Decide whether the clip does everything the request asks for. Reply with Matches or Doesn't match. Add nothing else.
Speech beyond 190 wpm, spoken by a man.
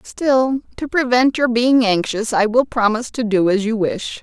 Doesn't match